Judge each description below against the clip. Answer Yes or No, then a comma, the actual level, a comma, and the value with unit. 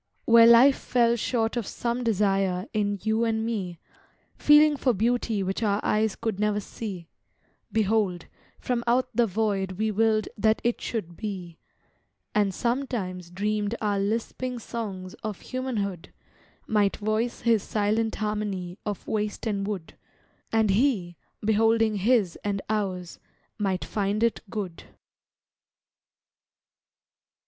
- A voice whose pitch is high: Yes, high, 215 Hz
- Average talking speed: No, slow, 125 wpm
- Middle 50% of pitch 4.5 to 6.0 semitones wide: No, average, 2.7 semitones